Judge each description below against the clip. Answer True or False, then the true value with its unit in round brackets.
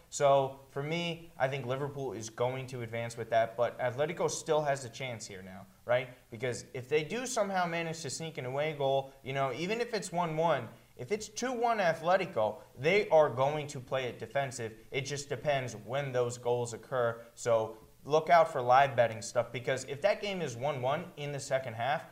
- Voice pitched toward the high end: False (135 Hz)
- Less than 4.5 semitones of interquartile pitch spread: False (4.8 semitones)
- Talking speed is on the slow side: False (205 wpm)